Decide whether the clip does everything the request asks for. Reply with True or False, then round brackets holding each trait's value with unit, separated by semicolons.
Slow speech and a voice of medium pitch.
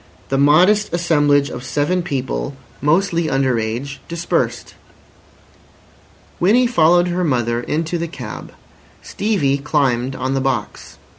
True (120 wpm; 145 Hz)